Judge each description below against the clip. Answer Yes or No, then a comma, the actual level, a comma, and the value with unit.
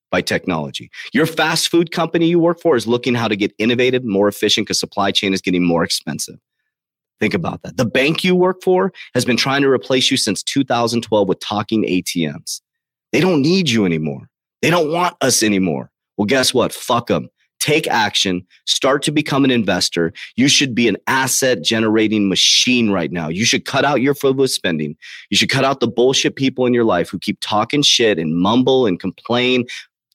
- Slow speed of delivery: No, average, 195 wpm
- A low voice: Yes, low, 120 Hz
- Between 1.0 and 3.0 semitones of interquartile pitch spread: No, wide, 5.4 semitones